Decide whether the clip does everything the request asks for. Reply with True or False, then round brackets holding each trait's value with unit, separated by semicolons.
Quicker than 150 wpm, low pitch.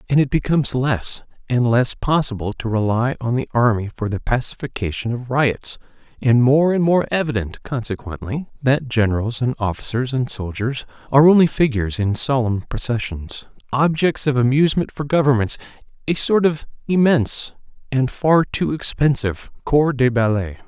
False (135 wpm; 130 Hz)